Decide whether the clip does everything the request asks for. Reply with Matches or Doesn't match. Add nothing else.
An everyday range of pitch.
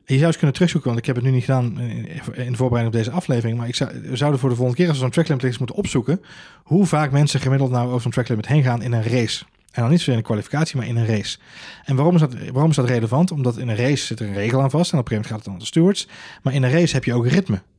Matches